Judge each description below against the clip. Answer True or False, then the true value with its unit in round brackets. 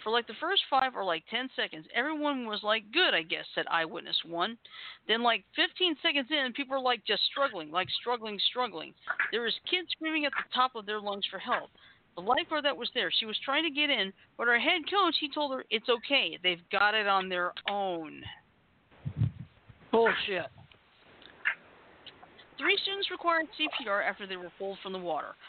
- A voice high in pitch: True (240 Hz)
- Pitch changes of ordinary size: False (7.0 semitones)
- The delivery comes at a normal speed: True (190 wpm)